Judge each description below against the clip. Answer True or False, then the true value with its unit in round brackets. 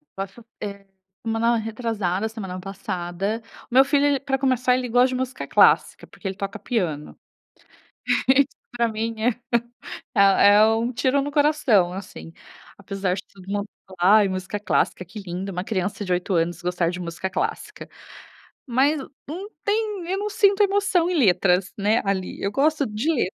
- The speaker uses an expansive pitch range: True (5.7 semitones)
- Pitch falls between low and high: False (215 Hz)